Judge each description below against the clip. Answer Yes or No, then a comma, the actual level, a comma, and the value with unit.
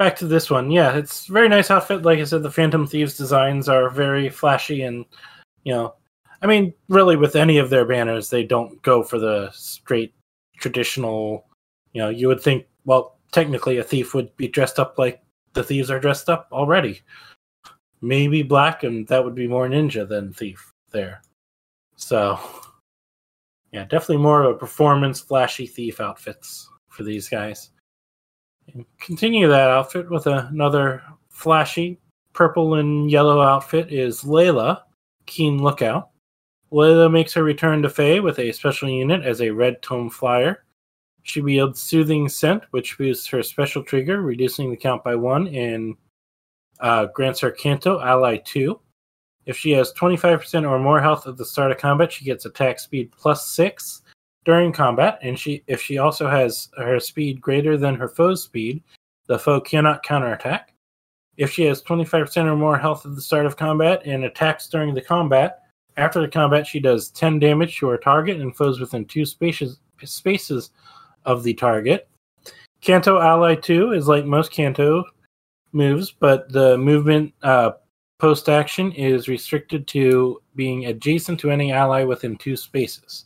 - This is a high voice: No, medium, 140 Hz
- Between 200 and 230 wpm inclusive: No, average, 165 wpm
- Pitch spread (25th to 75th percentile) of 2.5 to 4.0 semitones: Yes, average, 3.7 semitones